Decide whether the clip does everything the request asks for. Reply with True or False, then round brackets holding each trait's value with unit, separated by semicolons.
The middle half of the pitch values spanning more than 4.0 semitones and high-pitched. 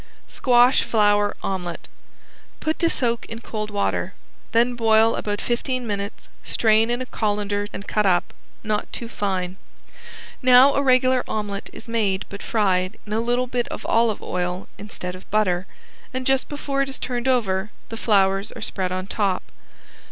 False (3.5 semitones; 215 Hz)